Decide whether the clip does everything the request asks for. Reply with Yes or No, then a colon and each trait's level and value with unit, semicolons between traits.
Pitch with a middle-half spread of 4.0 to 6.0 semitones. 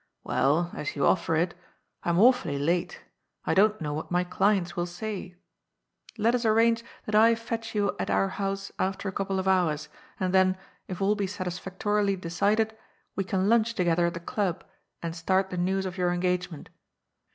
No: average, 3.0 semitones